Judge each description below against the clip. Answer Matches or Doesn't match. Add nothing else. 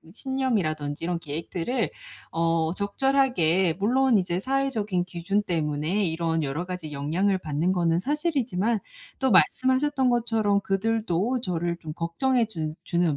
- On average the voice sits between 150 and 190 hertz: Matches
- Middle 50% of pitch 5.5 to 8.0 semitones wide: Matches